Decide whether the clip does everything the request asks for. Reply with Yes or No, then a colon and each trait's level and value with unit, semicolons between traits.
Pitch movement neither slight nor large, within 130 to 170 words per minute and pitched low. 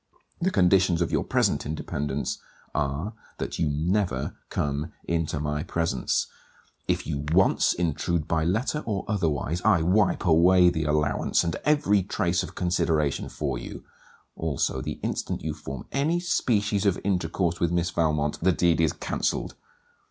Yes: average, 3.8 semitones; average, 150 wpm; very low, 85 Hz